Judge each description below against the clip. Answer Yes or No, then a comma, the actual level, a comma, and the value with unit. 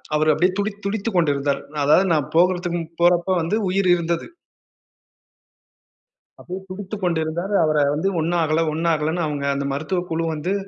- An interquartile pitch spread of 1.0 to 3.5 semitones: Yes, average, 3.0 semitones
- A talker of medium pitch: Yes, medium, 170 Hz